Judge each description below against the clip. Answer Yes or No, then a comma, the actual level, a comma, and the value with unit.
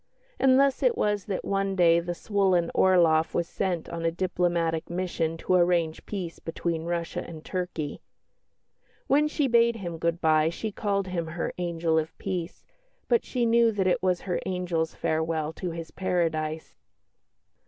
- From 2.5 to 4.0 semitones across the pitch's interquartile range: Yes, average, 2.9 semitones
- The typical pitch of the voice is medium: Yes, medium, 175 Hz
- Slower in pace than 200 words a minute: Yes, average, 165 wpm